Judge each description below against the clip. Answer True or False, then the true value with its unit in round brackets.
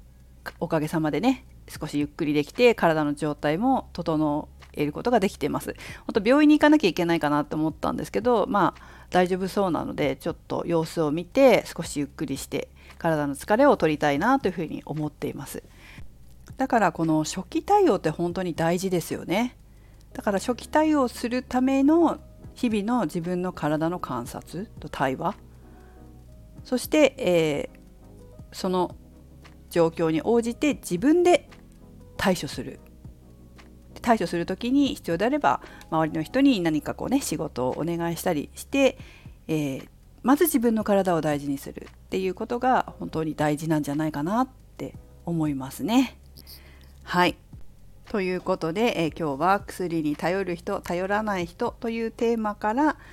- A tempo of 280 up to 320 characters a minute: True (315 characters per minute)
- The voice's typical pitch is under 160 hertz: False (170 Hz)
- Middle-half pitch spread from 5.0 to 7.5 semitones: False (7.9 semitones)